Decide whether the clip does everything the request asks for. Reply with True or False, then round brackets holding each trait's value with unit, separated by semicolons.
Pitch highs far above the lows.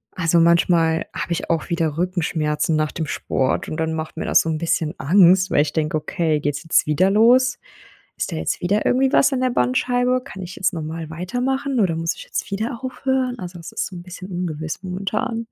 True (5.7 semitones)